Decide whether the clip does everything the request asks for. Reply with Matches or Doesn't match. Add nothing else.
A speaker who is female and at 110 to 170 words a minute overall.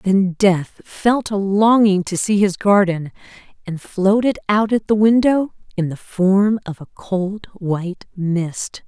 Matches